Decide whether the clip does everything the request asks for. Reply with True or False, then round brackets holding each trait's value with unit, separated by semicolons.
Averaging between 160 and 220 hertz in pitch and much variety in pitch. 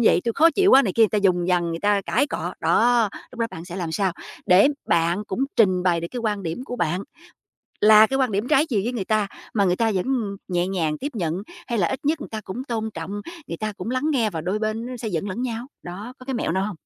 False (210 Hz; 5.0 semitones)